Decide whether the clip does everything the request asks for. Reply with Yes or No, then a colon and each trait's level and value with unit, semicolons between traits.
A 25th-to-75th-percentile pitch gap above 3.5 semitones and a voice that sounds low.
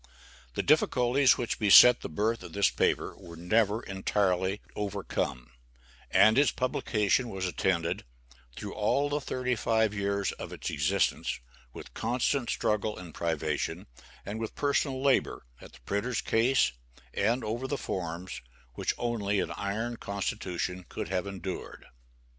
Yes: average, 4.3 semitones; low, 105 Hz